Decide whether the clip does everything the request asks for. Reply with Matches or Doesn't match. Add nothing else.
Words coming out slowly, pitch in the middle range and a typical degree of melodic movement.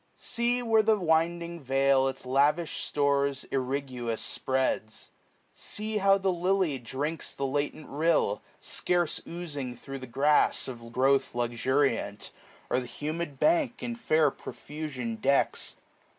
Matches